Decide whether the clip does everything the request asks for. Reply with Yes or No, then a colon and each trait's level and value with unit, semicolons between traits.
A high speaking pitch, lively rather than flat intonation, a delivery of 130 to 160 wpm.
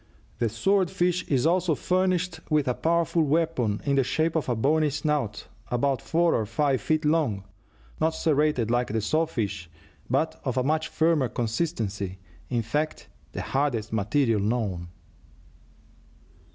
No: medium, 140 Hz; wide, 5.9 semitones; average, 150 wpm